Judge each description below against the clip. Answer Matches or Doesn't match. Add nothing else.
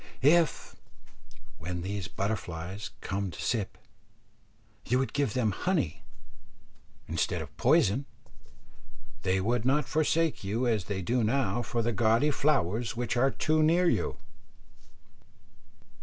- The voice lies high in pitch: Doesn't match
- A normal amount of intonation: Doesn't match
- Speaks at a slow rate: Matches